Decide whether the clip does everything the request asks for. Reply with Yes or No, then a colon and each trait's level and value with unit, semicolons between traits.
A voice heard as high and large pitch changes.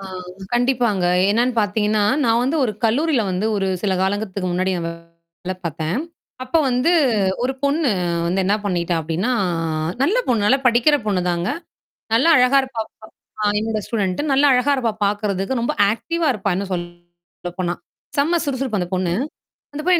Yes: high, 210 Hz; wide, 5.8 semitones